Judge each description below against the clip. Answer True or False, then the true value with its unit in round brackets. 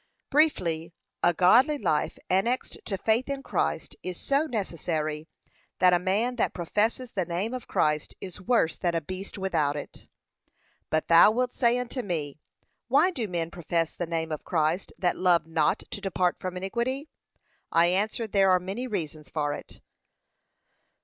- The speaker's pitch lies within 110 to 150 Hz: False (185 Hz)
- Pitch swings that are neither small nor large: False (5.9 semitones)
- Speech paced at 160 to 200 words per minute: True (165 wpm)